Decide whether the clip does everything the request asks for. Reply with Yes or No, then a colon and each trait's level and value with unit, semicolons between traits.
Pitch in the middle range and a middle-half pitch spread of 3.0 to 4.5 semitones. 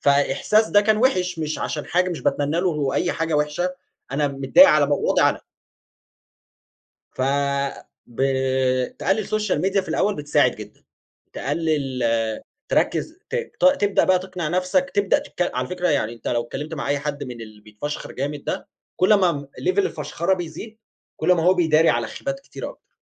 No: medium, 165 Hz; average, 5.2 semitones